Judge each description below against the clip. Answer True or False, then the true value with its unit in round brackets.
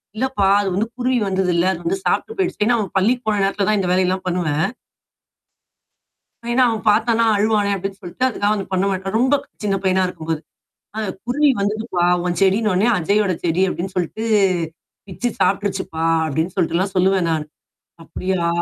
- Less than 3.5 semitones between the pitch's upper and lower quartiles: True (3.0 semitones)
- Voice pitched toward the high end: True (195 Hz)